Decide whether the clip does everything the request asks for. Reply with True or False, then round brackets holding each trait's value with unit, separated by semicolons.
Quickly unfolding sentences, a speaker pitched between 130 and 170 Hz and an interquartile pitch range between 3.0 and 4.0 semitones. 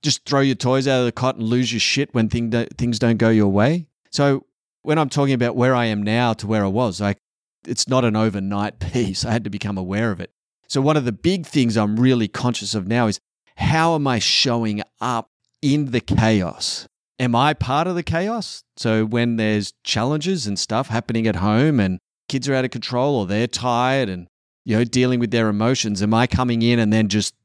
False (225 wpm; 120 Hz; 3.5 semitones)